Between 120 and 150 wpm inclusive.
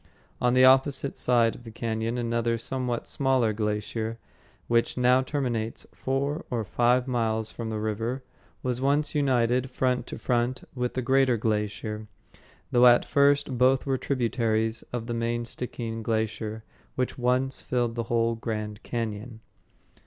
Yes: average, 145 wpm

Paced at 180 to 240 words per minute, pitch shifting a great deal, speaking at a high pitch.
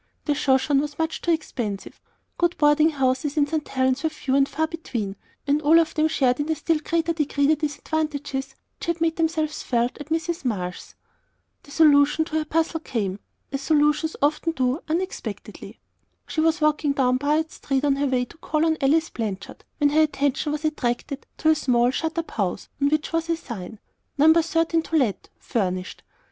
No: average, 190 wpm; average, 3.1 semitones; very high, 295 Hz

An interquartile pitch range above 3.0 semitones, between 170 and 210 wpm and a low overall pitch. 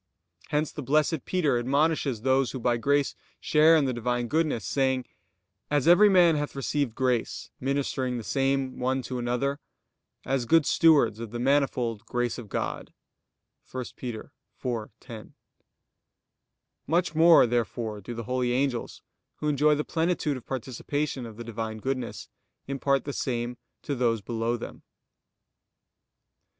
No: average, 3.4 semitones; average, 140 wpm; low, 130 Hz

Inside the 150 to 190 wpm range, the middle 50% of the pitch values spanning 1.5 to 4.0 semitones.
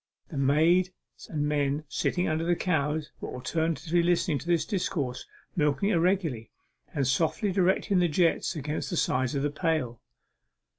Yes: average, 155 wpm; average, 3.7 semitones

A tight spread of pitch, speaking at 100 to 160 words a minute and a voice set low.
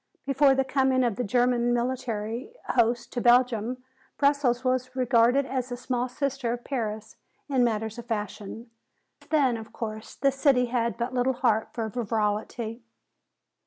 No: narrow, 2.1 semitones; average, 155 wpm; high, 245 Hz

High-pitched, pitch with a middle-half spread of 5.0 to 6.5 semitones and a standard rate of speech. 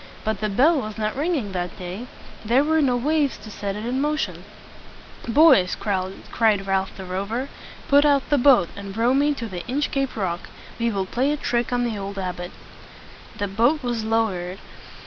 Yes: high, 225 Hz; wide, 5.6 semitones; average, 185 wpm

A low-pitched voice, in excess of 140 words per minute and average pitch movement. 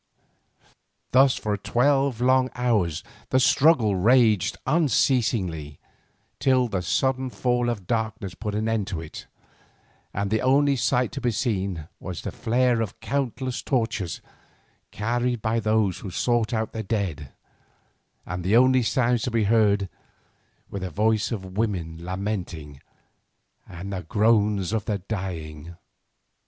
No: low, 110 Hz; slow, 135 wpm; average, 4.5 semitones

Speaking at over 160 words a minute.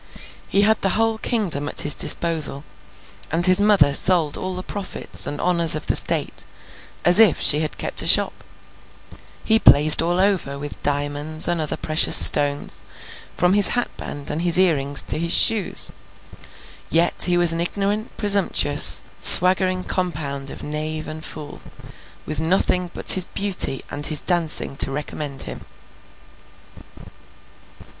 No: average, 150 wpm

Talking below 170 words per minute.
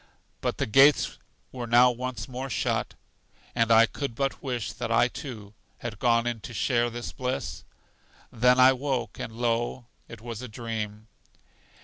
Yes: average, 160 wpm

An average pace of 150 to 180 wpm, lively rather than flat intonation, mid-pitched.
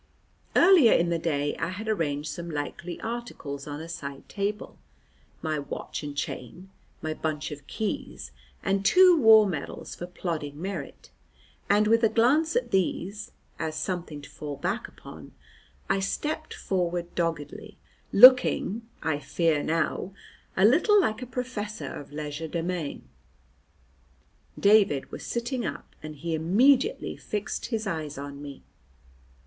No: average, 140 wpm; wide, 6.4 semitones; medium, 175 Hz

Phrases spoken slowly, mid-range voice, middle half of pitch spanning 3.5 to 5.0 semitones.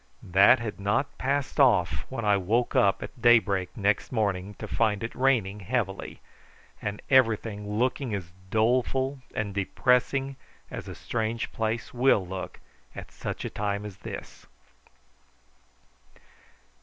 No: slow, 130 wpm; low, 110 Hz; average, 3.9 semitones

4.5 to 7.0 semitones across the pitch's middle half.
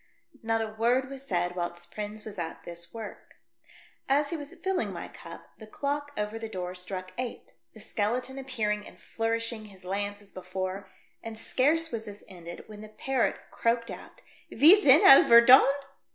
Yes: average, 4.8 semitones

